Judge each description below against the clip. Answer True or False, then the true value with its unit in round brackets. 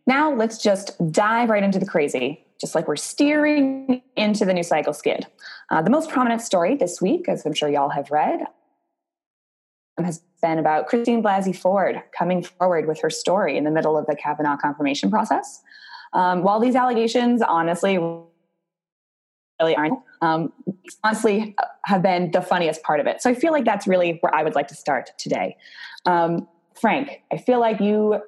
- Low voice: False (185 Hz)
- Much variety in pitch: True (5.7 semitones)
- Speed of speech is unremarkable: True (180 wpm)